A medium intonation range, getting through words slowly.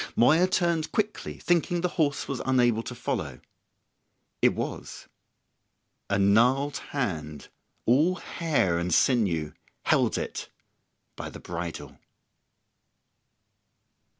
No: wide, 8.5 semitones; slow, 100 wpm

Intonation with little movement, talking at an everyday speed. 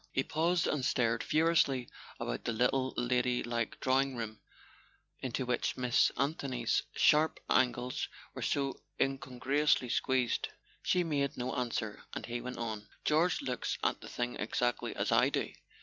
Yes: narrow, 2.3 semitones; average, 150 wpm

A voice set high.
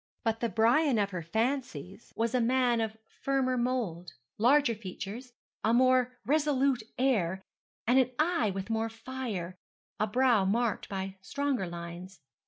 Yes: high, 230 Hz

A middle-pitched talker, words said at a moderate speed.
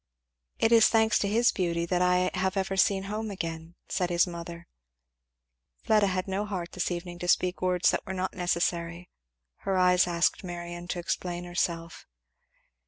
Yes: medium, 180 Hz; average, 170 wpm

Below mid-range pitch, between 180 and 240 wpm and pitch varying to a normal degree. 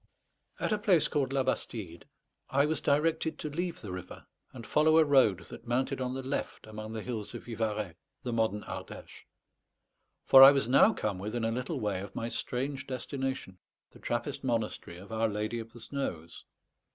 Yes: low, 120 Hz; average, 185 wpm; average, 4.3 semitones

